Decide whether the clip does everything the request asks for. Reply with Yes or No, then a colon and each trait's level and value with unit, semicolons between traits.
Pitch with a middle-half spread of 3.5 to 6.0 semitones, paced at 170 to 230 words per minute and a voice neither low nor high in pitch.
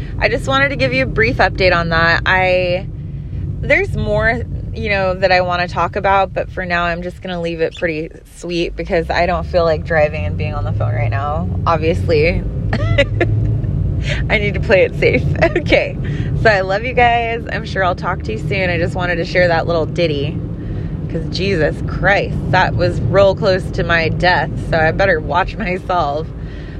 Yes: average, 5.2 semitones; average, 200 wpm; medium, 165 Hz